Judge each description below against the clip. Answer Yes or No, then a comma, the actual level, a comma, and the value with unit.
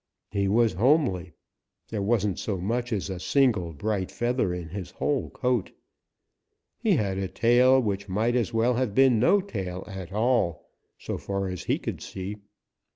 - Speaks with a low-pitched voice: Yes, low, 105 Hz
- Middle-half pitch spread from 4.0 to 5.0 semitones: Yes, average, 4.3 semitones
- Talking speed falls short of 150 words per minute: No, average, 165 wpm